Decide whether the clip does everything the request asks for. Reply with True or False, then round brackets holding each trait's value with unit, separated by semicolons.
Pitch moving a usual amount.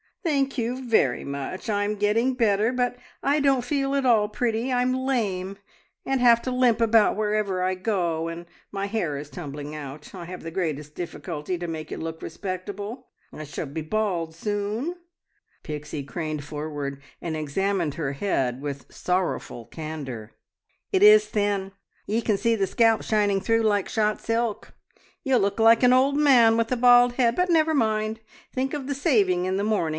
False (6.7 semitones)